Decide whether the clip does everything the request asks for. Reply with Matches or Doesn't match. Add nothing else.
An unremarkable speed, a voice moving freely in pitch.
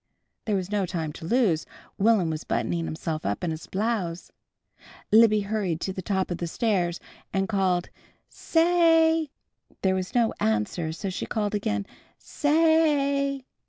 Matches